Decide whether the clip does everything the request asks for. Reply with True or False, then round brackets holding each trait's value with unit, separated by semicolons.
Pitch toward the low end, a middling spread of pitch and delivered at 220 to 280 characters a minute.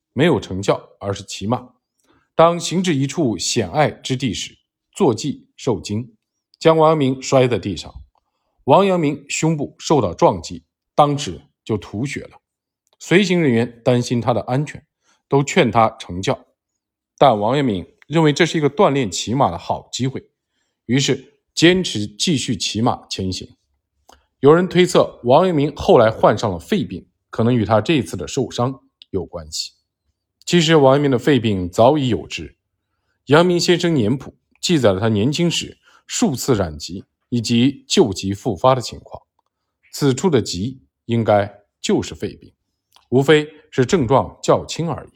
False (130 Hz; 6.6 semitones; 225 characters per minute)